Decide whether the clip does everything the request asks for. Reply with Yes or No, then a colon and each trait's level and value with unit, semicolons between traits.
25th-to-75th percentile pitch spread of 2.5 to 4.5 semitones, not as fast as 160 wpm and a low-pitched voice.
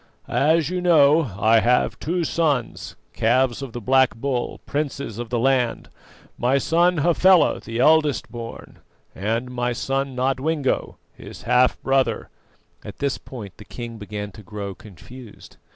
Yes: average, 3.8 semitones; average, 150 wpm; low, 130 Hz